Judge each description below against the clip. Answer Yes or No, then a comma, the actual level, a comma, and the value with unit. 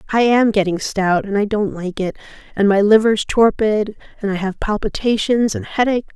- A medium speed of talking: Yes, average, 185 wpm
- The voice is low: No, high, 205 Hz